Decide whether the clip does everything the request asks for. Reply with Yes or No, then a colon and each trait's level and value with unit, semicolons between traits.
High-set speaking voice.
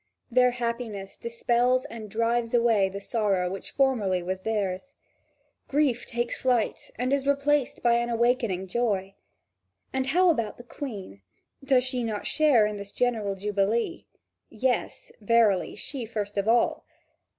Yes: high, 235 Hz